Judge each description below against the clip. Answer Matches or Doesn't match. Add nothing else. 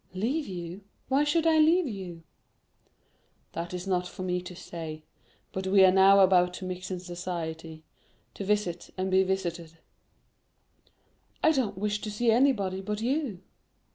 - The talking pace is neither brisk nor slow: Matches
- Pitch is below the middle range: Doesn't match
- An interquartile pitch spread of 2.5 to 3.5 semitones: Matches